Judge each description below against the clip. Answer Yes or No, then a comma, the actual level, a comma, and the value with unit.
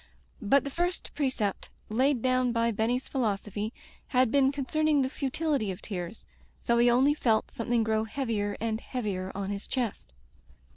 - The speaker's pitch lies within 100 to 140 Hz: No, high, 235 Hz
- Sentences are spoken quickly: No, average, 160 wpm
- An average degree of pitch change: Yes, average, 4.0 semitones